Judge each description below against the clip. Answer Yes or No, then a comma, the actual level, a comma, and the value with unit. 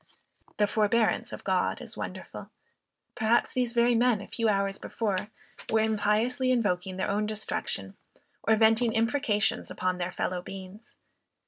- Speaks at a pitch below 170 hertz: No, high, 220 Hz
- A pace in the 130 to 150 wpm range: Yes, average, 140 wpm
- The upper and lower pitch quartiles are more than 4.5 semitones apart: No, average, 2.8 semitones